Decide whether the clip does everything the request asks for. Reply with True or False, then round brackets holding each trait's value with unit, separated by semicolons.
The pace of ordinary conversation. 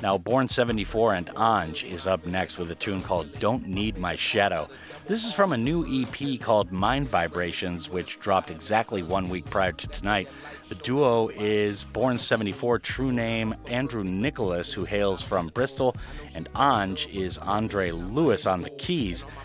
True (165 wpm)